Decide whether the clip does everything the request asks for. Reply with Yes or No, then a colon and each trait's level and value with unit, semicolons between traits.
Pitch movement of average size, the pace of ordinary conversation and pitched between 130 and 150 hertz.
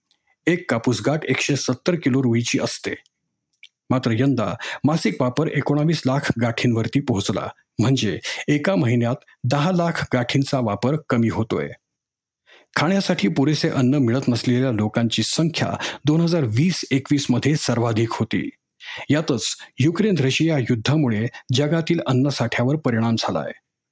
Yes: average, 3.9 semitones; average, 120 wpm; low, 135 Hz